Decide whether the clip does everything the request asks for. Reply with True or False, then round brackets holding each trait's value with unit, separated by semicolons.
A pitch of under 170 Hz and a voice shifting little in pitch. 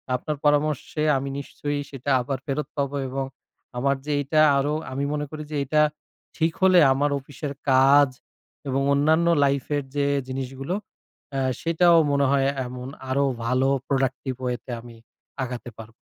True (140 Hz; 1.9 semitones)